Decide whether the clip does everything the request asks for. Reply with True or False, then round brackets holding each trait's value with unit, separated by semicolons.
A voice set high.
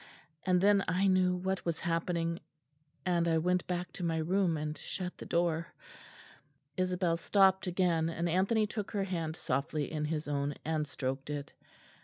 False (170 Hz)